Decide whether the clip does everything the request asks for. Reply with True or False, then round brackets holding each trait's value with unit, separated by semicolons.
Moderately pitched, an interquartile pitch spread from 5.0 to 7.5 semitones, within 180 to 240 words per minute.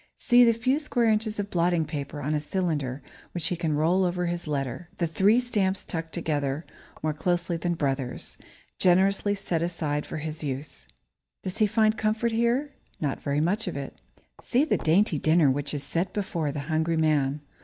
True (170 Hz; 5.4 semitones; 185 wpm)